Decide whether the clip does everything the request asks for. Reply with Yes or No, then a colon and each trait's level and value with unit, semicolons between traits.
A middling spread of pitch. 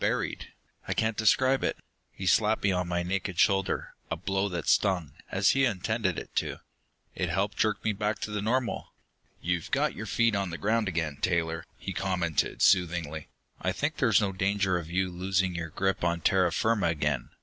Yes: average, 3.4 semitones